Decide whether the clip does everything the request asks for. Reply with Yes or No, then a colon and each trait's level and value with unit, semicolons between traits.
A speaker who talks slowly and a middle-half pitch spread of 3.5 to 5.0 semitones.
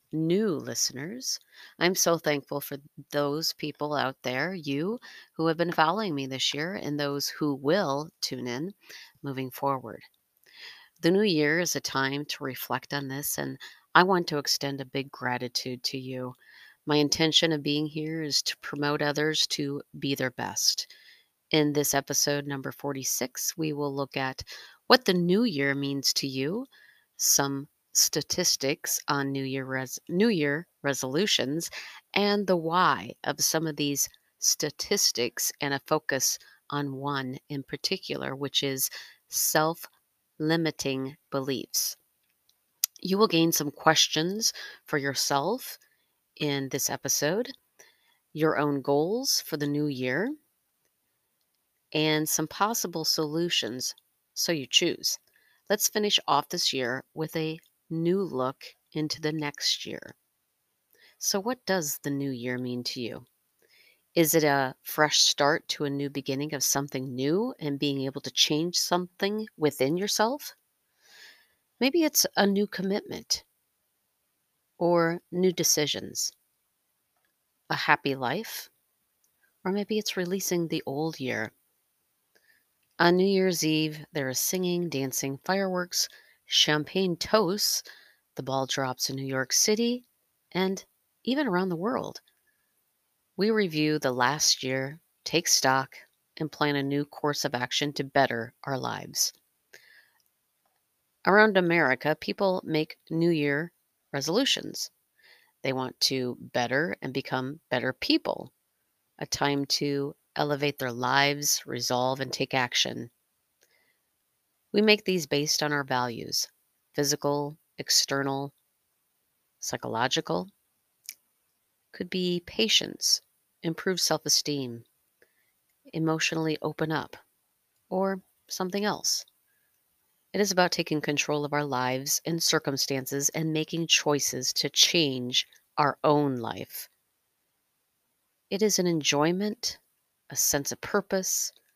Yes: slow, 125 wpm; average, 4.2 semitones